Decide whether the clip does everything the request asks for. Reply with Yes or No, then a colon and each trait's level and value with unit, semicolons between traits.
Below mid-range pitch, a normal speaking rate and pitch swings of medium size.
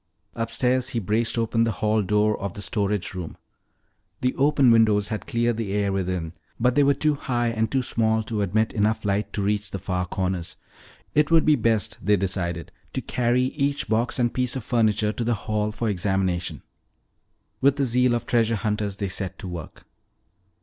Yes: low, 110 Hz; average, 190 wpm; average, 3.2 semitones